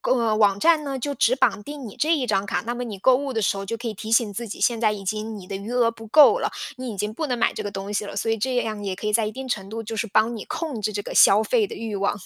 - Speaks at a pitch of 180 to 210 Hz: No, high, 225 Hz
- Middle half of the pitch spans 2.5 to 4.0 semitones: Yes, average, 3.3 semitones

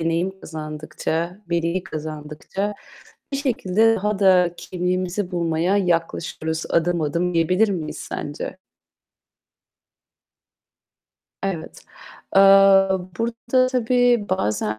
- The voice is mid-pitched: Yes, medium, 180 Hz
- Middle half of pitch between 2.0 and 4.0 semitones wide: Yes, average, 3.7 semitones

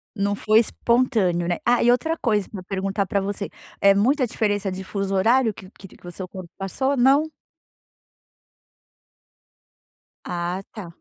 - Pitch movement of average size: Yes, average, 3.9 semitones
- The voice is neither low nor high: No, high, 200 Hz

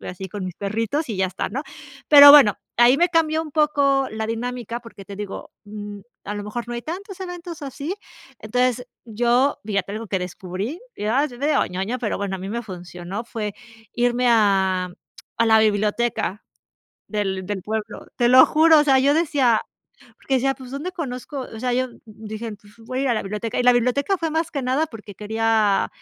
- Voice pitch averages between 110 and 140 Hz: No, high, 235 Hz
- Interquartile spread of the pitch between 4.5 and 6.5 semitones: Yes, average, 4.8 semitones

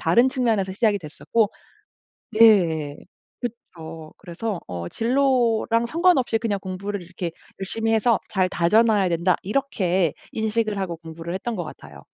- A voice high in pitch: Yes, high, 200 Hz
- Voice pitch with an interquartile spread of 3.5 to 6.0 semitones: Yes, average, 5.1 semitones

